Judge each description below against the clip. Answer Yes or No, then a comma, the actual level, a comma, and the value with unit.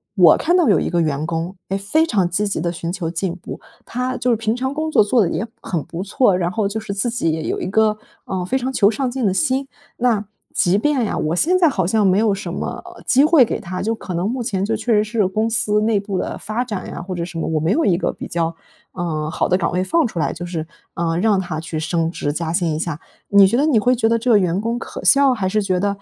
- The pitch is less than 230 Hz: Yes, high, 200 Hz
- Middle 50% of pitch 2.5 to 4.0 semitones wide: No, average, 5.0 semitones